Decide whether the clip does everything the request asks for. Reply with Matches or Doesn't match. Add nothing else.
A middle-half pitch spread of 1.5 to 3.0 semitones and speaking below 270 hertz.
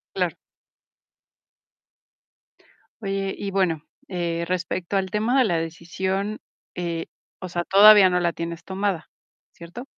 Matches